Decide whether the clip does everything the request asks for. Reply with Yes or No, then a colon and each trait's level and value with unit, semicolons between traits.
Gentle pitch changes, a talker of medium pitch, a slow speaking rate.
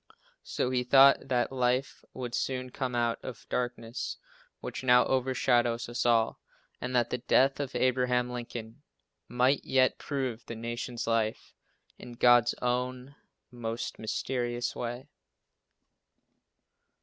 No: narrow, 1.3 semitones; low, 125 Hz; slow, 125 wpm